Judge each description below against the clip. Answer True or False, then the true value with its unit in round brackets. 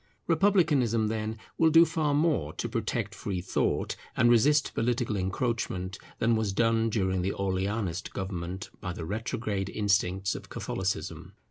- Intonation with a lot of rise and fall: False (4.0 semitones)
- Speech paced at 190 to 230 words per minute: False (140 wpm)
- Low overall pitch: True (110 Hz)